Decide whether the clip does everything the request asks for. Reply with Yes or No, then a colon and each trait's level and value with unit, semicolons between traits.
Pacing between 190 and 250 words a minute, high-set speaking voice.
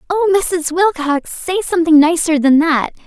No: average, 155 wpm; very high, 335 Hz